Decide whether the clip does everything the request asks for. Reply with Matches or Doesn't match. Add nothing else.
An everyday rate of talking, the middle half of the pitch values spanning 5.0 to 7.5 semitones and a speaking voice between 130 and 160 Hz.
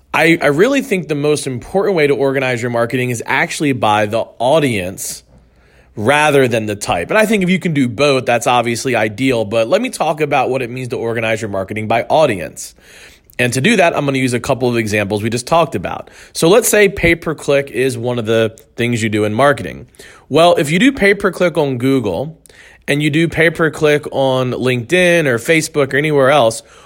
Doesn't match